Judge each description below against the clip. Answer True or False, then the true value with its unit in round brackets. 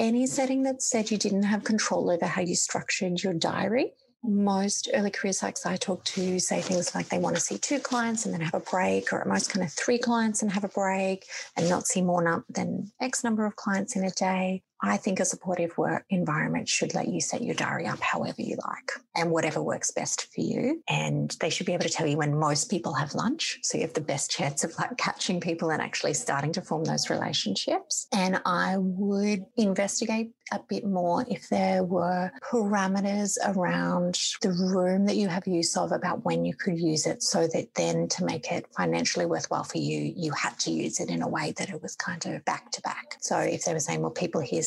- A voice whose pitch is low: False (190 Hz)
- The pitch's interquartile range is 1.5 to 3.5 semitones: True (3.2 semitones)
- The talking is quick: True (225 wpm)